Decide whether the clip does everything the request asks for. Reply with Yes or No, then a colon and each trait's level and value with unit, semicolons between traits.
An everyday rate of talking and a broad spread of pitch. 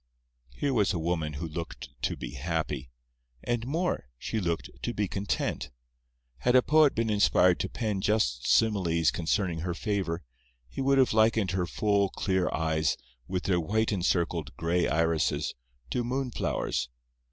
No: average, 150 wpm; average, 5.0 semitones